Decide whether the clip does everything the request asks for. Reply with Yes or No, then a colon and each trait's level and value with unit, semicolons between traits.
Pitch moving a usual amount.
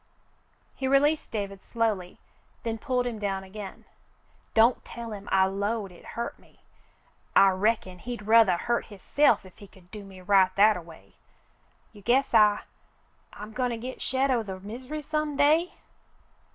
Yes: average, 4.0 semitones